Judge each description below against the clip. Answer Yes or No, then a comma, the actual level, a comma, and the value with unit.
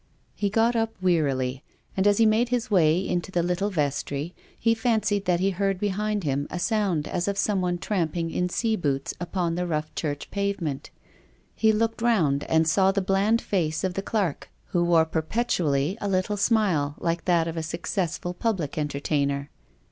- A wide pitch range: No, average, 4.5 semitones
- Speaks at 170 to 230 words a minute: Yes, average, 180 wpm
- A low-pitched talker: No, medium, 180 Hz